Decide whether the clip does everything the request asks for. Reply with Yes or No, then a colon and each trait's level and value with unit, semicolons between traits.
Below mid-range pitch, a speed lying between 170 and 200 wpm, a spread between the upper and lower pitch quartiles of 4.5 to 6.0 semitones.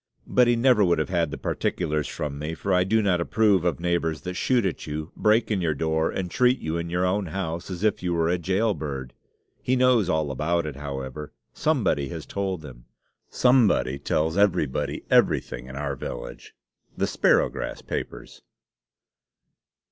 Yes: very low, 85 Hz; average, 175 wpm; average, 4.8 semitones